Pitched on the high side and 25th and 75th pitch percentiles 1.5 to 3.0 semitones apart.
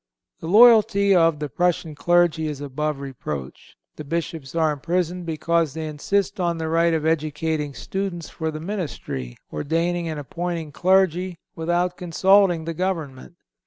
No: medium, 165 Hz; average, 2.7 semitones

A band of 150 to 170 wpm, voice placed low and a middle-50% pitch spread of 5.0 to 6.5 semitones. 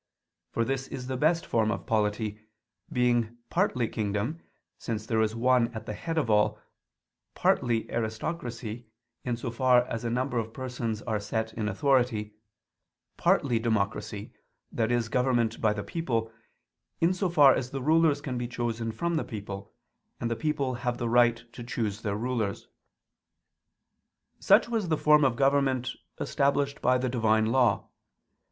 No: average, 155 wpm; low, 120 Hz; average, 3.0 semitones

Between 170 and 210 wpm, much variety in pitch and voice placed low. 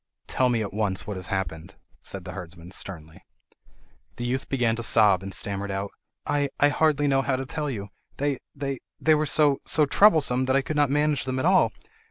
Yes: average, 185 wpm; wide, 6.5 semitones; low, 130 Hz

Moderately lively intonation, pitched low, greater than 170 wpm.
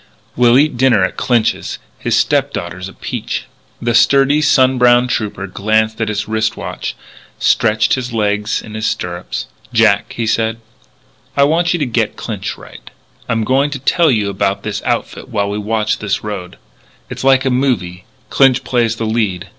Yes: average, 3.8 semitones; low, 115 Hz; average, 180 wpm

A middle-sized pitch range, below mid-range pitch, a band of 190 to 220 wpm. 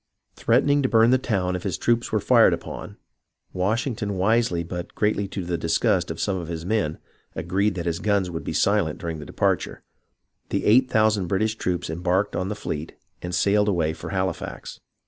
Yes: average, 3.8 semitones; very low, 95 Hz; average, 195 wpm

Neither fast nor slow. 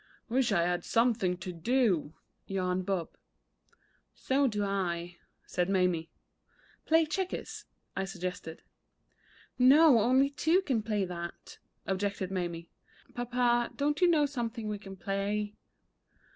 No: slow, 120 wpm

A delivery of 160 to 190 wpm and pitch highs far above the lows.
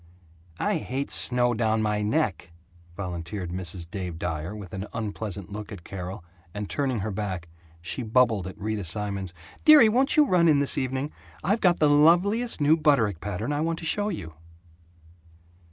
Yes: average, 170 wpm; wide, 7.6 semitones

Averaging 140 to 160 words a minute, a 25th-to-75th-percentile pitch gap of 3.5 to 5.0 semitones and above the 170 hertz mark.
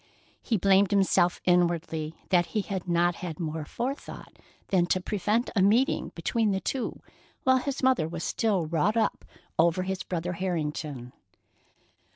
Yes: average, 150 wpm; average, 3.8 semitones; medium, 185 Hz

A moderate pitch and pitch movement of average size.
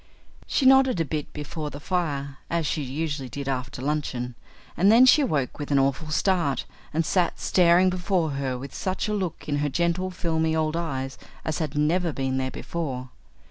Yes: medium, 155 Hz; average, 4.0 semitones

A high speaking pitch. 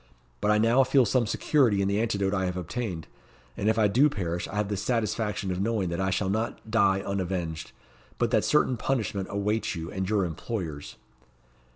No: low, 100 Hz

